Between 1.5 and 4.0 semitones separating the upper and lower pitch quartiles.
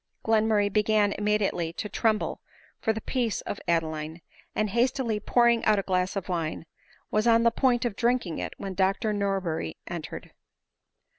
Yes: average, 3.2 semitones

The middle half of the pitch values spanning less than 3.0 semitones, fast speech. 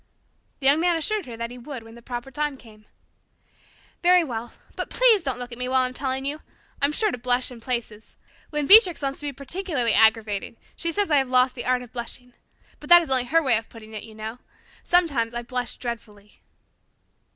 No: average, 4.1 semitones; fast, 220 wpm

